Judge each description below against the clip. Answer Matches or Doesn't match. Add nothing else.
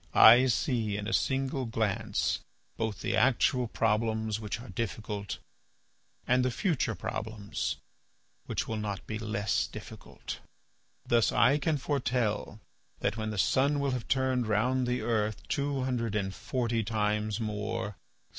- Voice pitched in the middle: Doesn't match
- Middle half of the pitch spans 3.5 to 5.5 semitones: Doesn't match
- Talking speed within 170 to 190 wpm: Doesn't match